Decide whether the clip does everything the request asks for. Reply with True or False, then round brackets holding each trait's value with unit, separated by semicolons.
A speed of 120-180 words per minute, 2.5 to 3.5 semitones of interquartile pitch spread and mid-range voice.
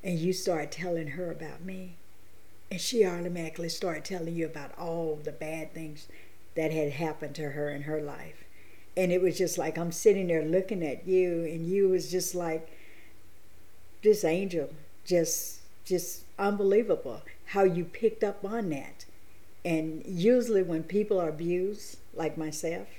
True (160 wpm; 3.0 semitones; 170 Hz)